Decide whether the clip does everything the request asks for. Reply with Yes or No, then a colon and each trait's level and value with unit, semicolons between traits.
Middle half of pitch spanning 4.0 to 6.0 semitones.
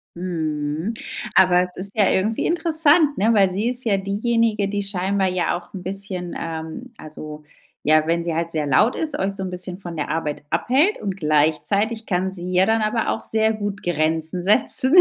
Yes: average, 4.5 semitones